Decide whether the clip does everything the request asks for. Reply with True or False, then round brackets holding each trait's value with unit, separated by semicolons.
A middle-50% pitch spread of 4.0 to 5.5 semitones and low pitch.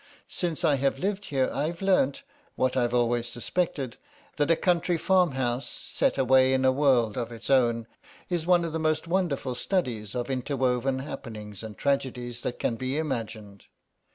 True (4.7 semitones; 130 Hz)